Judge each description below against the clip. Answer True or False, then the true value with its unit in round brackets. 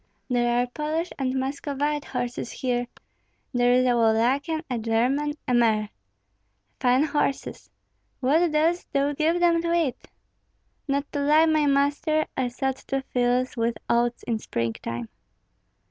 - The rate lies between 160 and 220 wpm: False (140 wpm)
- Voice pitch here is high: True (265 Hz)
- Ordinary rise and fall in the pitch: True (3.5 semitones)